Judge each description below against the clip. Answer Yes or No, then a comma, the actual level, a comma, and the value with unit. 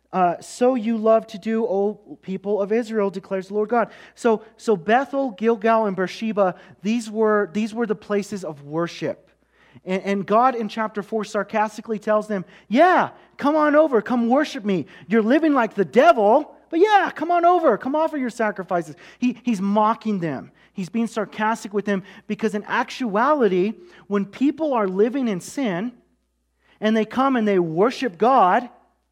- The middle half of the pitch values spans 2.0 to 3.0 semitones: No, average, 3.4 semitones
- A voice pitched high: Yes, high, 220 Hz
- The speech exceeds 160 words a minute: Yes, average, 170 wpm